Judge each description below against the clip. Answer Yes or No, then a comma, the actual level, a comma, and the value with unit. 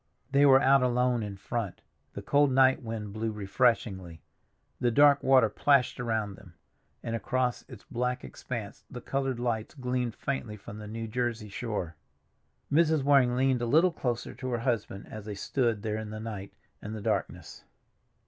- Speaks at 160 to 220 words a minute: Yes, average, 170 wpm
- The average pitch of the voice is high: No, low, 120 Hz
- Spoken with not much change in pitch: No, average, 3.3 semitones